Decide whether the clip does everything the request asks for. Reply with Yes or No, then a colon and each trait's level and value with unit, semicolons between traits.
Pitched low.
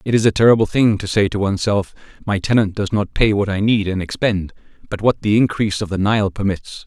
Yes: low, 105 Hz